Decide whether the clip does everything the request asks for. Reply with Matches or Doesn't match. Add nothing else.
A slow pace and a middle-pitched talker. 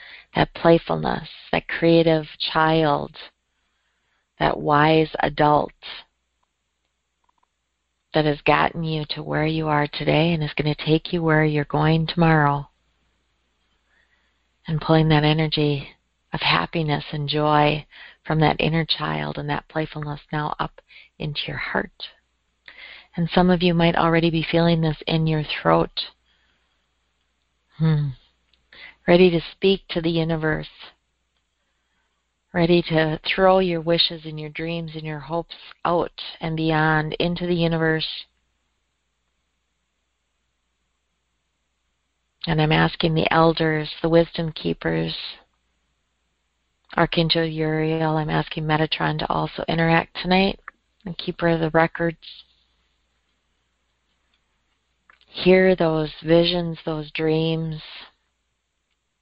Matches